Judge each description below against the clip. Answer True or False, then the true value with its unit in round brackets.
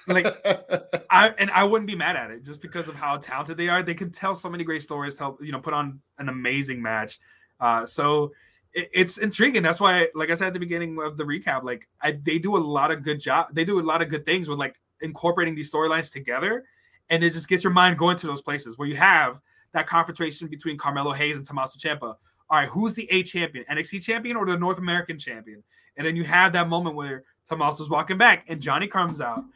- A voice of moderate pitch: True (160 Hz)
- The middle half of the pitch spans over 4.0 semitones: False (3.5 semitones)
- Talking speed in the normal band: False (240 wpm)